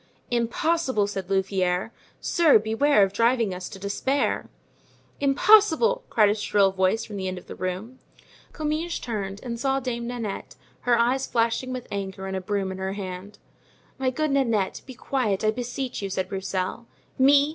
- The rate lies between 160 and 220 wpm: Yes, average, 170 wpm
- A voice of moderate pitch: No, high, 225 Hz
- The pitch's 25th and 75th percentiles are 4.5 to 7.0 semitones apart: Yes, average, 5.2 semitones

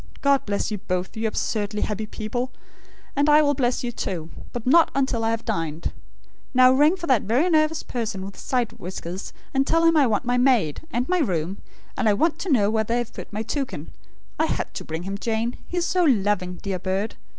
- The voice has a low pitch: No, high, 230 Hz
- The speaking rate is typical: No, fast, 215 wpm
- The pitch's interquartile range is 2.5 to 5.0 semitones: No, wide, 5.4 semitones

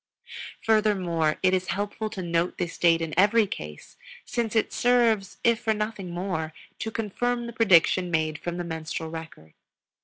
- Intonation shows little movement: No, average, 4.9 semitones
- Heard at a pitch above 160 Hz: Yes, medium, 185 Hz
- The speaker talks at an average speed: Yes, average, 160 wpm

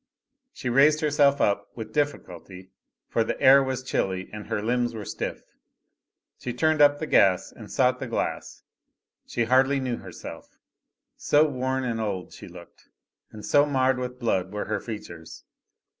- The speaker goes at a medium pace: Yes, average, 160 wpm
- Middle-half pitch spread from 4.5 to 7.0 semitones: Yes, average, 4.9 semitones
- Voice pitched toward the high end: No, low, 125 Hz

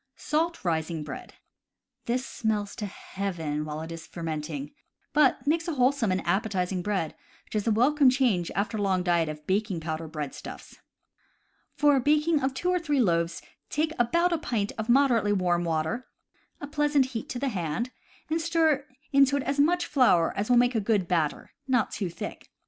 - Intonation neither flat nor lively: No, wide, 8.3 semitones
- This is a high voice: Yes, high, 220 Hz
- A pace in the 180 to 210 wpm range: Yes, average, 185 wpm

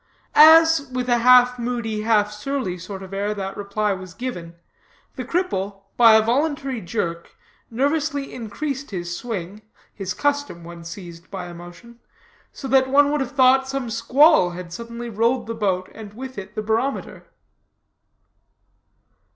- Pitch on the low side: No, high, 230 Hz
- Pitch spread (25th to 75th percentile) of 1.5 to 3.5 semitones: No, wide, 5.5 semitones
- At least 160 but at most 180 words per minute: No, average, 150 wpm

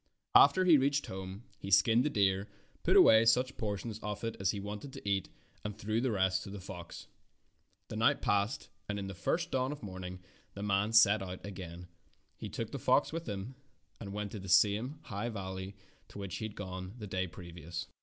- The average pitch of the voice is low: Yes, low, 100 Hz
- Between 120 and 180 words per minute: No, fast, 205 wpm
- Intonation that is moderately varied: Yes, average, 3.0 semitones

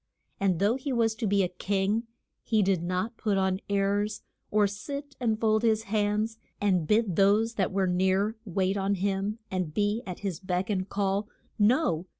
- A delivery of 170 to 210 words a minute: Yes, average, 180 wpm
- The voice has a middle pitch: No, high, 200 Hz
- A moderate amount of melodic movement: No, narrow, 2.3 semitones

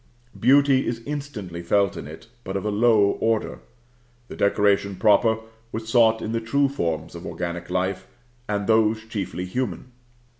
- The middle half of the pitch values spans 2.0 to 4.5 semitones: Yes, average, 3.3 semitones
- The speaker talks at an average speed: Yes, average, 155 wpm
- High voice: No, low, 105 Hz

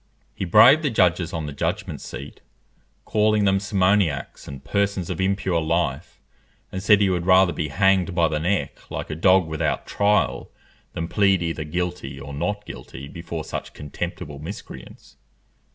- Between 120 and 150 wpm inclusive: No, average, 160 wpm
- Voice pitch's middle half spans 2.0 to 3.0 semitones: No, average, 3.8 semitones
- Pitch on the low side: Yes, very low, 90 Hz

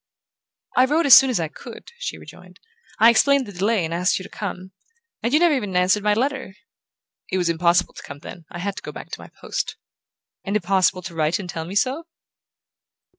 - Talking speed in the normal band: No, fast, 215 wpm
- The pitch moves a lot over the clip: Yes, wide, 6.2 semitones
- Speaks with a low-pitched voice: No, high, 195 Hz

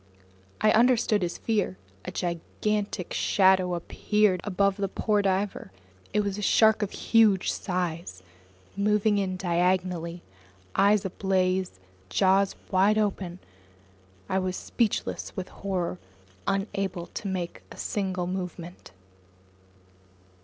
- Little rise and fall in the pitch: Yes, narrow, 2.3 semitones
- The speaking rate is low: Yes, slow, 110 wpm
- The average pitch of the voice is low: No, high, 190 Hz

